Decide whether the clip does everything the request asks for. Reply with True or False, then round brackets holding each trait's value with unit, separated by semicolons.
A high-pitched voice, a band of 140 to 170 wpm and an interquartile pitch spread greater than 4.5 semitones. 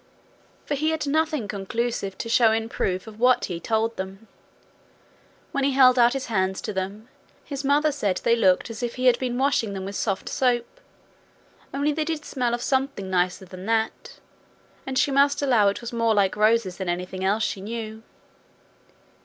False (230 Hz; 185 wpm; 5.0 semitones)